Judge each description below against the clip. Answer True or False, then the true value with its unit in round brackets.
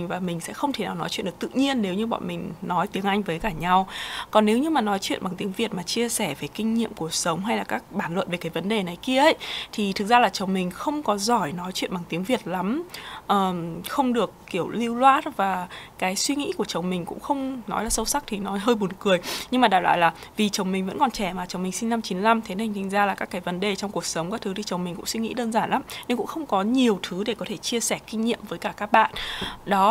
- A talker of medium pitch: False (200 Hz)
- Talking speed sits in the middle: False (295 wpm)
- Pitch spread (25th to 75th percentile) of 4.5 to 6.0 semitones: False (3.9 semitones)